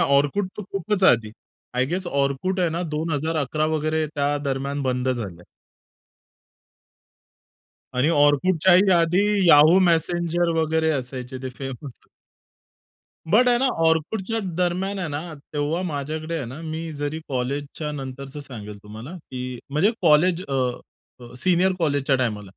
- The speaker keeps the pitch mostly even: No, average, 4.2 semitones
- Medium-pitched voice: Yes, medium, 150 Hz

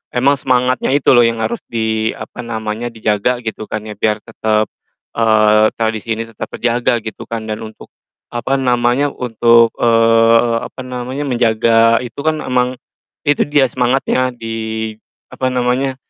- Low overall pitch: Yes, low, 115 Hz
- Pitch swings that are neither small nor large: No, narrow, 2.1 semitones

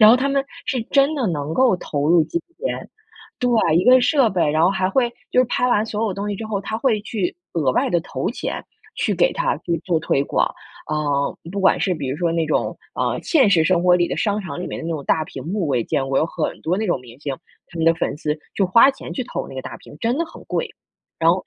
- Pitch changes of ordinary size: No, wide, 6.7 semitones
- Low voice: No, medium, 185 Hz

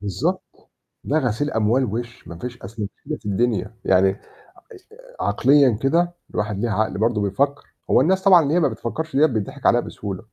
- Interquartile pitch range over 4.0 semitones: Yes, wide, 5.5 semitones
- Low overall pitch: Yes, low, 120 Hz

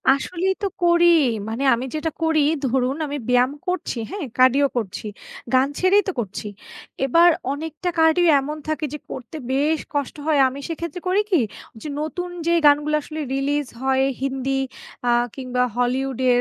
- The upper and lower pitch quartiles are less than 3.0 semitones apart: No, average, 3.8 semitones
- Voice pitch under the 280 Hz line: No, very high, 290 Hz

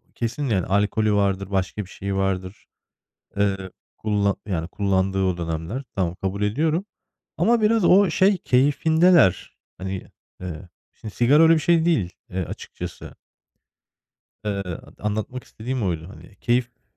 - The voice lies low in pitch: Yes, low, 105 Hz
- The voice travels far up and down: Yes, wide, 6.4 semitones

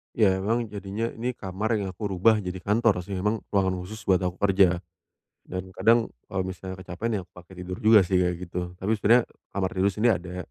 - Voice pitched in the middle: No, very low, 95 Hz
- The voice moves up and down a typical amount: Yes, average, 3.0 semitones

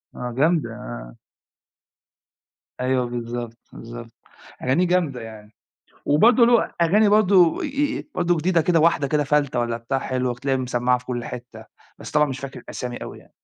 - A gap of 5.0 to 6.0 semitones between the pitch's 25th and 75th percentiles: Yes, wide, 5.6 semitones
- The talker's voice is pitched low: Yes, low, 130 Hz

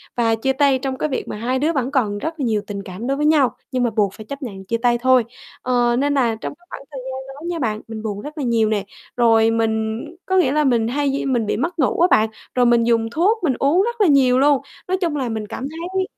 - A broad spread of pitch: No, average, 4.3 semitones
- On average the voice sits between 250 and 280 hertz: Yes, very high, 255 Hz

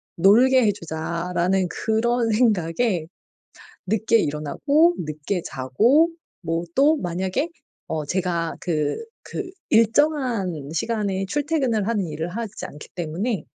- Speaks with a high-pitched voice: Yes, high, 195 Hz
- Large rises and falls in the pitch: Yes, wide, 6.1 semitones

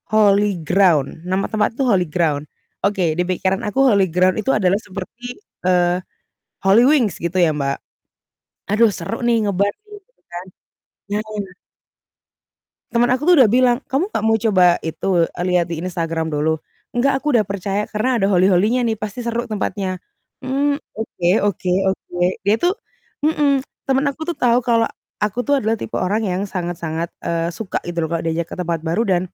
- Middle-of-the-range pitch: No, high, 200 Hz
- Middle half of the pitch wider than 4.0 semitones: Yes, average, 5.1 semitones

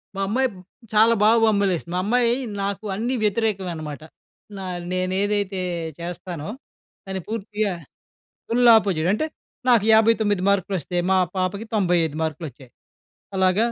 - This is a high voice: Yes, high, 195 Hz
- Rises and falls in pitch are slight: No, average, 3.3 semitones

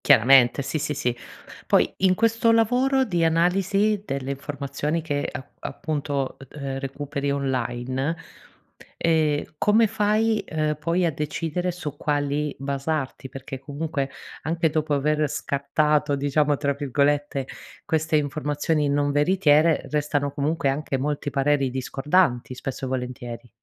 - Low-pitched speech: No, medium, 145 Hz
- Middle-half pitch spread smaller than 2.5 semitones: No, average, 2.8 semitones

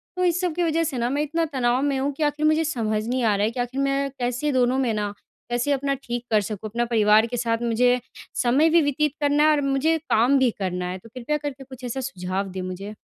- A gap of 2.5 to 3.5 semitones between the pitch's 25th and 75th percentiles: No, average, 4.2 semitones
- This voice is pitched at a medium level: No, very high, 255 Hz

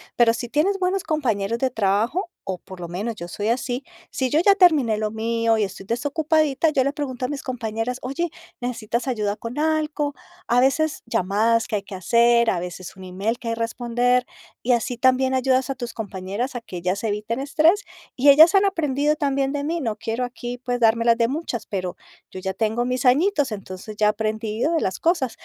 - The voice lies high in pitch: Yes, high, 240 Hz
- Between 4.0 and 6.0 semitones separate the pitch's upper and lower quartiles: Yes, average, 4.4 semitones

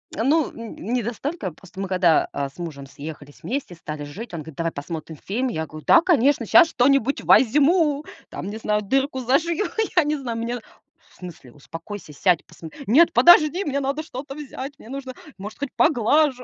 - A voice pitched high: Yes, high, 235 Hz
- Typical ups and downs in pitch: No, wide, 8.6 semitones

